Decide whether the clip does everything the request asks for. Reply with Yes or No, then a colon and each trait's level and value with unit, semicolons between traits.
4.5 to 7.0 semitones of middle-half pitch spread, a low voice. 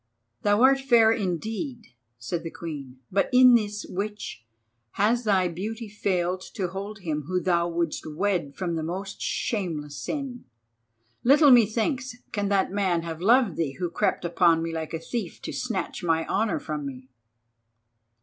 No: average, 4.9 semitones; high, 190 Hz